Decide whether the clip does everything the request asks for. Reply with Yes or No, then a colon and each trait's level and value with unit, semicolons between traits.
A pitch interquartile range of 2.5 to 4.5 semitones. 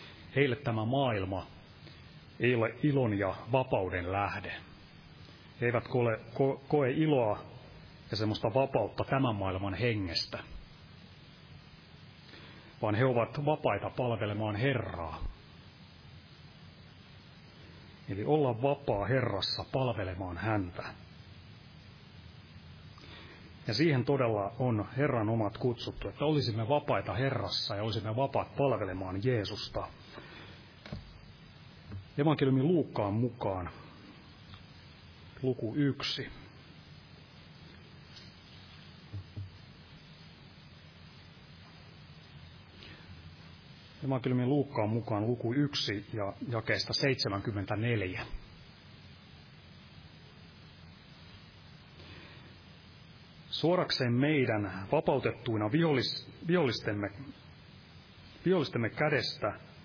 No: average, 5.2 semitones